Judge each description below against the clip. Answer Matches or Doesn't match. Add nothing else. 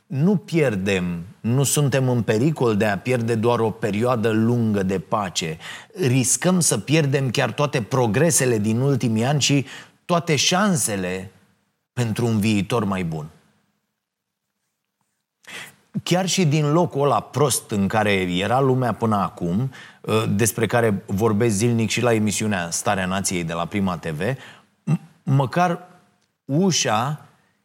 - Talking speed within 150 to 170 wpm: Doesn't match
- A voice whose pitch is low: Matches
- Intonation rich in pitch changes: Matches